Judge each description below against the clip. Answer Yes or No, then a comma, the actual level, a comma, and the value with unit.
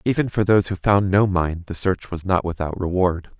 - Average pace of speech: No, fast, 230 wpm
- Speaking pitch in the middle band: No, very low, 95 Hz